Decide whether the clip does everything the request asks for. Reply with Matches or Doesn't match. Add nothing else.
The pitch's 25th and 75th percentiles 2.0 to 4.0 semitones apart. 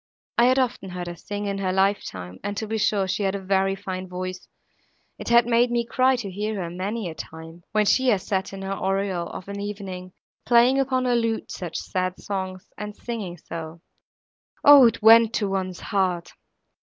Matches